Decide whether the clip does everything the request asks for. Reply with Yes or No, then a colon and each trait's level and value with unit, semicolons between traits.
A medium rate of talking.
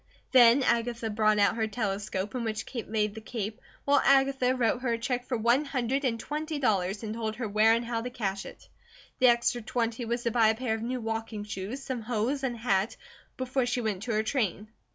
No: fast, 225 wpm